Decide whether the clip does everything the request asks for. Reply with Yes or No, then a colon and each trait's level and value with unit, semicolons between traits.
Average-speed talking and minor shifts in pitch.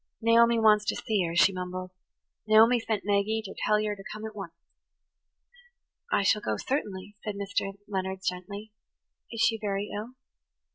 Yes: average, 160 wpm; narrow, 2.3 semitones